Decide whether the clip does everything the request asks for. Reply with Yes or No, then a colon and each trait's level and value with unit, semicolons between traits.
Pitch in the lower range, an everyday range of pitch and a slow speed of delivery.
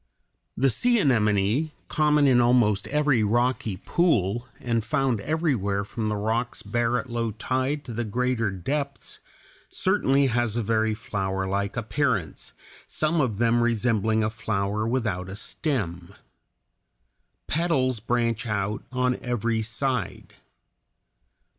Yes: low, 115 Hz; average, 3.6 semitones; slow, 120 wpm